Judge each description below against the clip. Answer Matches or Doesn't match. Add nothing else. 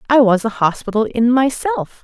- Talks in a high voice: Matches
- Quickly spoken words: Doesn't match